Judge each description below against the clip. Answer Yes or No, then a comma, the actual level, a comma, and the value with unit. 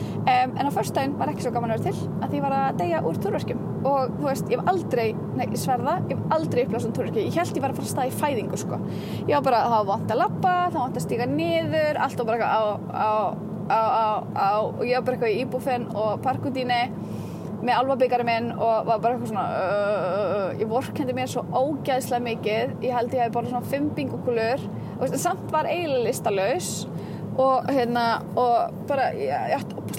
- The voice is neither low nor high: No, high, 245 Hz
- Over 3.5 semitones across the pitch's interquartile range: No, narrow, 2.6 semitones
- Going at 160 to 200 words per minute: Yes, average, 180 wpm